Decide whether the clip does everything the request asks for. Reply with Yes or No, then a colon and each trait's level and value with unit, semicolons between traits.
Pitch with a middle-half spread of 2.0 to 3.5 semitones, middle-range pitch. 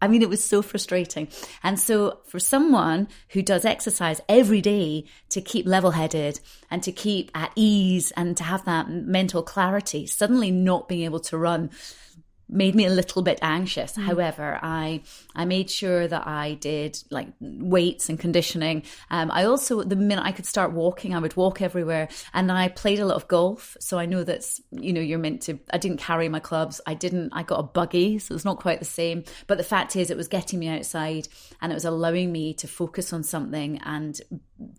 Yes: average, 3.0 semitones; medium, 175 Hz